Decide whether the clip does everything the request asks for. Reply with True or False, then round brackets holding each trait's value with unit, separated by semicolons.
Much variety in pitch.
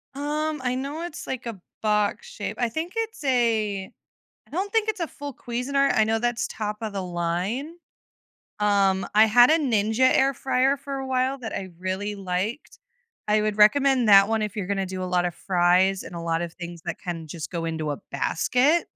True (6.2 semitones)